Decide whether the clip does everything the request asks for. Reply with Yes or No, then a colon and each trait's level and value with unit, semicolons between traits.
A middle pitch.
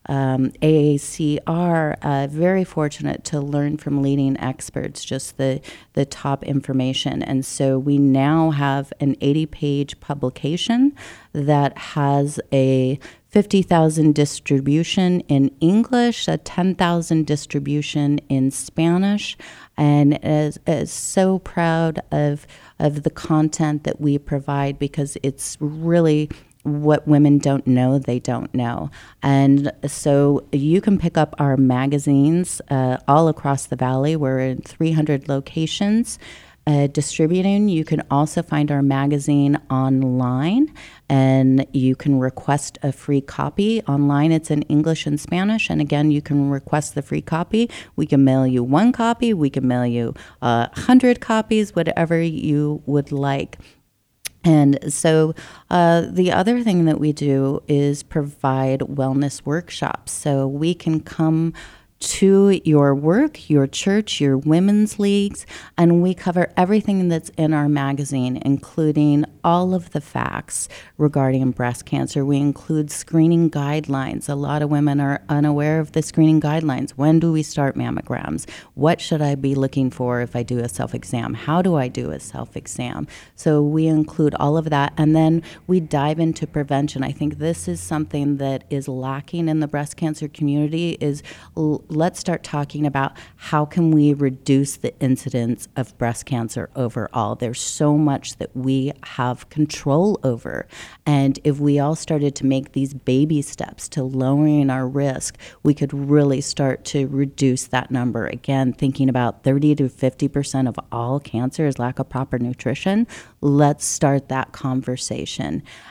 Yes: medium, 145 Hz